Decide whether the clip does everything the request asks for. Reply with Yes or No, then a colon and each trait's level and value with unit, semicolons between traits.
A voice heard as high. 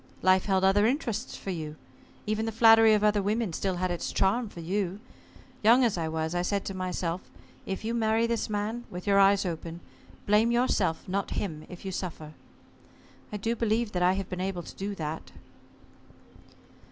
Yes: high, 195 Hz